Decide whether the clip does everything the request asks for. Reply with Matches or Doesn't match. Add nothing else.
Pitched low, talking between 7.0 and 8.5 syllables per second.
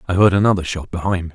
Matches